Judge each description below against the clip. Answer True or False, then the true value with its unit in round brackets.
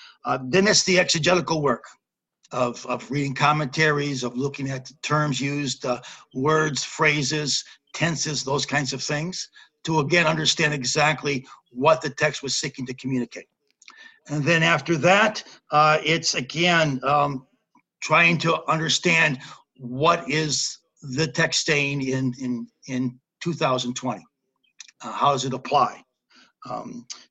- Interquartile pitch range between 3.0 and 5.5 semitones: True (3.4 semitones)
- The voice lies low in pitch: False (150 Hz)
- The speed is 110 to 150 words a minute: True (135 wpm)